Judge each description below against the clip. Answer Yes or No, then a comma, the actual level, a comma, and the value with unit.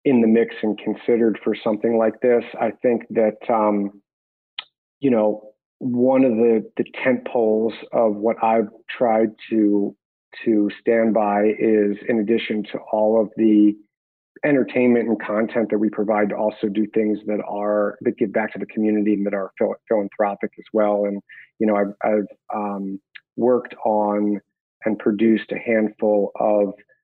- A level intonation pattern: Yes, narrow, 1.4 semitones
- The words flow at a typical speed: Yes, average, 160 wpm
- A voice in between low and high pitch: No, low, 110 Hz